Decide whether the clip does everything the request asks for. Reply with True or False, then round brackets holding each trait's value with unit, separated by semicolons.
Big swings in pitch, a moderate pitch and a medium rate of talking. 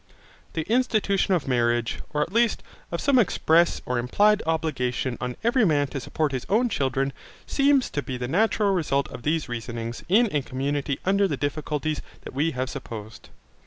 True (7.5 semitones; 150 Hz; 175 wpm)